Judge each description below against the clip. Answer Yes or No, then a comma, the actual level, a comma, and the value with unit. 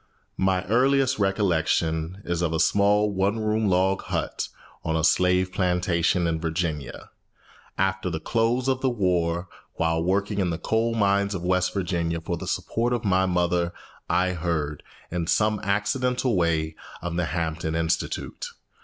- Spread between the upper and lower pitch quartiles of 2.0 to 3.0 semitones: No, average, 3.5 semitones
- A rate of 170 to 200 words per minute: No, average, 155 wpm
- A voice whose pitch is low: Yes, very low, 90 Hz